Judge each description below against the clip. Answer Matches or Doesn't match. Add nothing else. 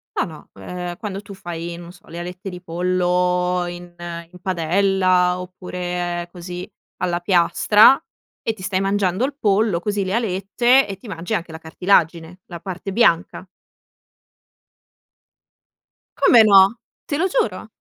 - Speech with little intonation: Matches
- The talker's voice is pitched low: Doesn't match